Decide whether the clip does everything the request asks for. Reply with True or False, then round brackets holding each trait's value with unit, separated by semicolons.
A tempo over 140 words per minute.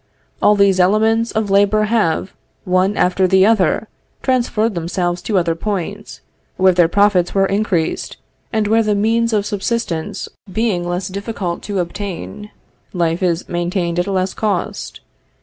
True (150 wpm)